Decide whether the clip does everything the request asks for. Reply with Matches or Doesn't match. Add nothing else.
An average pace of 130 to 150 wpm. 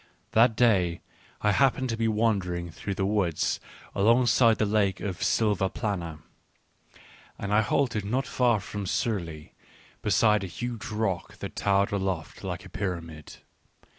Matches